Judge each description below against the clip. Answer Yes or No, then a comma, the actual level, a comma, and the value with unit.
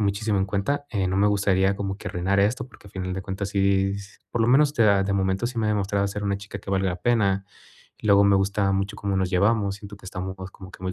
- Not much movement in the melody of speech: Yes, narrow, 1.2 semitones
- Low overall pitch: Yes, low, 100 Hz